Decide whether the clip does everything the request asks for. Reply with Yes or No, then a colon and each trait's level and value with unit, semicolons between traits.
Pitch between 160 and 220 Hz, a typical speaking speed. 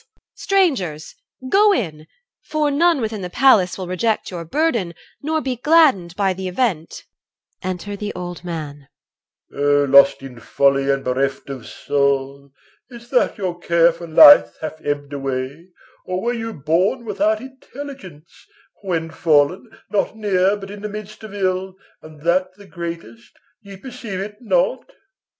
Yes: medium, 185 Hz; average, 160 wpm